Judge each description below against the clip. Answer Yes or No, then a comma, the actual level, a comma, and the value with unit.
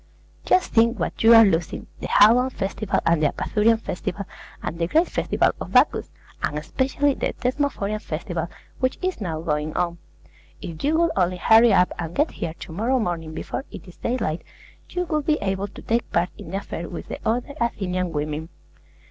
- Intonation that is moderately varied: No, wide, 6.4 semitones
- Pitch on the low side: No, high, 200 Hz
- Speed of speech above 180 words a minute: Yes, average, 190 wpm